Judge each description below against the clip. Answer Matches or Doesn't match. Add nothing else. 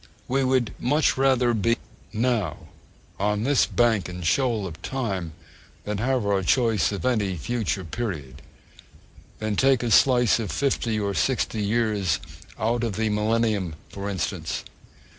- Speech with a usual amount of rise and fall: Matches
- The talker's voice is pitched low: Matches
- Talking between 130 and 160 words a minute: Matches